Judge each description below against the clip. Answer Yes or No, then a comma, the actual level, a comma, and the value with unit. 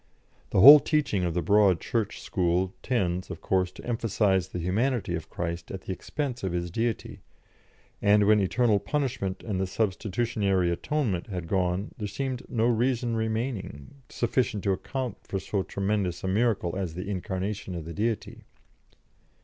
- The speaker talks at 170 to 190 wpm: No, average, 160 wpm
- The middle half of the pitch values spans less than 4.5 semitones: Yes, average, 4.1 semitones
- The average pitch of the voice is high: No, low, 100 Hz